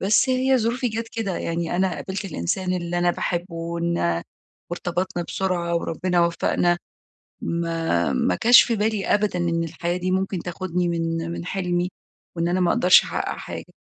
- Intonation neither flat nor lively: No, narrow, 2.2 semitones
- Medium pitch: Yes, medium, 175 Hz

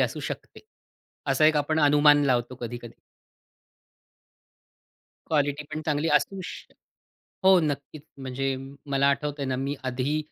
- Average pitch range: No, narrow, 2.2 semitones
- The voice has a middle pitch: Yes, medium, 145 Hz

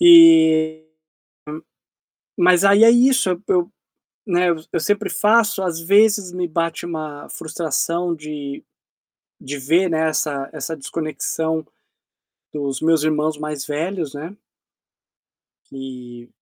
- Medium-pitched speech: Yes, medium, 160 Hz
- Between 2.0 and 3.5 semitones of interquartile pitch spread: No, average, 3.9 semitones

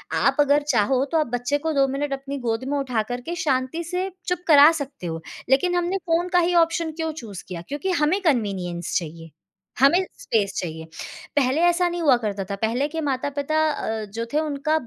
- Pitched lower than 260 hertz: No, very high, 280 Hz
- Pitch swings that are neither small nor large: No, wide, 5.9 semitones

